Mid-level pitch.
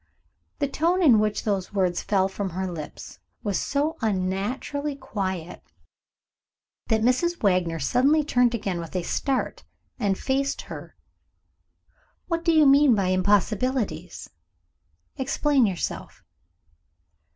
No: high, 215 Hz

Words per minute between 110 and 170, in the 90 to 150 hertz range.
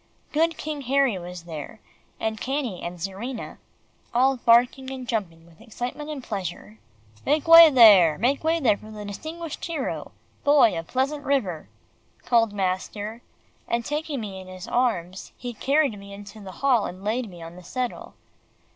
No: average, 165 wpm; high, 230 Hz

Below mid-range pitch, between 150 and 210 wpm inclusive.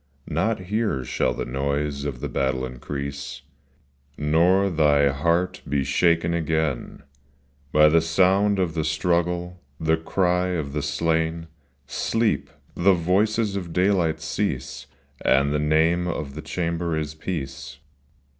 No: very low, 80 Hz; slow, 135 wpm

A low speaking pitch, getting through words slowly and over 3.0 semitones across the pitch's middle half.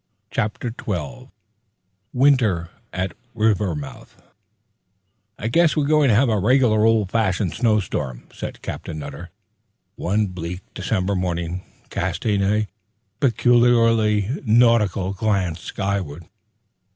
Yes: low, 105 Hz; slow, 105 wpm; average, 4.0 semitones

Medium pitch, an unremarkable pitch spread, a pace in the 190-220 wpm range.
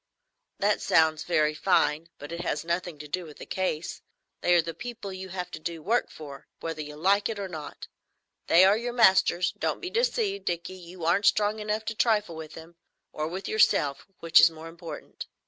Yes: medium, 175 Hz; average, 4.1 semitones; average, 200 wpm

